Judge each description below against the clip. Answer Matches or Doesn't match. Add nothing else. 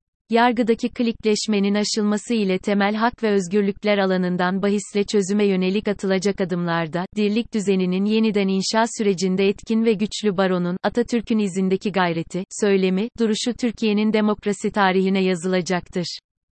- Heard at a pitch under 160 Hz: Doesn't match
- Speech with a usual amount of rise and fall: Doesn't match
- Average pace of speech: Matches